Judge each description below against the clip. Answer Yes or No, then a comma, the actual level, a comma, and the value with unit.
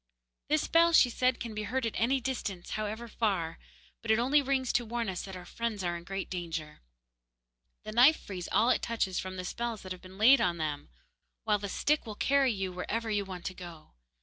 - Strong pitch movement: No, average, 4.6 semitones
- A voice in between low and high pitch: No, high, 215 Hz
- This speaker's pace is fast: Yes, fast, 220 wpm